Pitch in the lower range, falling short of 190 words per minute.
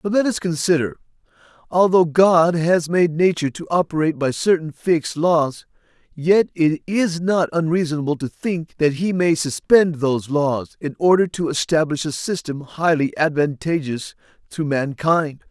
No: medium, 160 Hz; average, 145 wpm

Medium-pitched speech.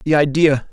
Yes: medium, 145 Hz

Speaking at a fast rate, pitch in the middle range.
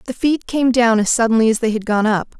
No: fast, 275 wpm; high, 230 Hz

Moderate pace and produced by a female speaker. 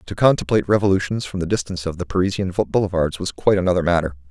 No: average, 195 wpm; male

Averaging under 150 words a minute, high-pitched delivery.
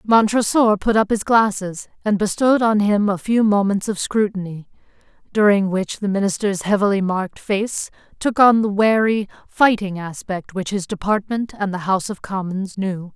No: average, 165 wpm; high, 200 Hz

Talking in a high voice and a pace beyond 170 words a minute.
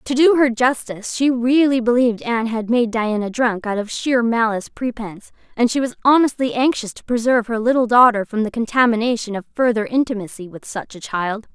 Yes: high, 235 Hz; average, 190 wpm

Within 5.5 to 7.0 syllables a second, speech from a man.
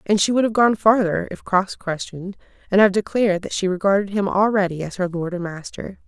No: 5.8 syllables/s; female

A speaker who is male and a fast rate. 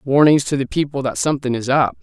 Yes: male; fast, 235 wpm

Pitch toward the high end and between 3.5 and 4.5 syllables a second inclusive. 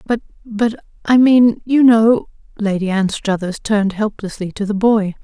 Yes: high, 215 Hz; 4.4 syllables/s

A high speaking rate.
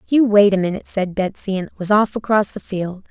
Yes: fast, 230 wpm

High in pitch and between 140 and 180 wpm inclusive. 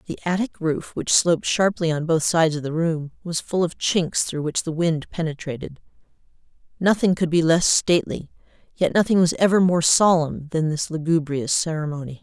No: medium, 165 Hz; average, 175 wpm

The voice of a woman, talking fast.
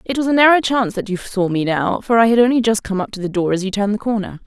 Yes: female; fast, 335 wpm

